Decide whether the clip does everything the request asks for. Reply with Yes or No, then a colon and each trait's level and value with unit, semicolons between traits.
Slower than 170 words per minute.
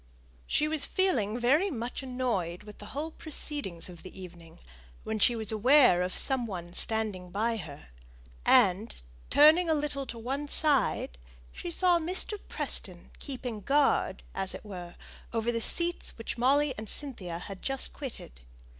Yes: average, 155 wpm